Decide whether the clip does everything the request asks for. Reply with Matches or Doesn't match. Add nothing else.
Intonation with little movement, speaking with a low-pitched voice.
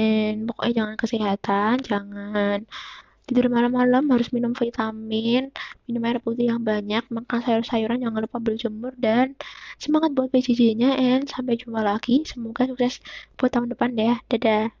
Doesn't match